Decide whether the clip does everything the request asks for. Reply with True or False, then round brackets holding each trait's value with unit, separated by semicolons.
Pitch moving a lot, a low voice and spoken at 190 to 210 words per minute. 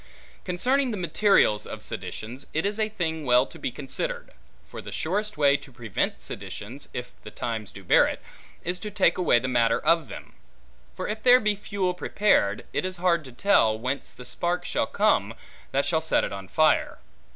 False (8.4 semitones; 160 Hz; 195 wpm)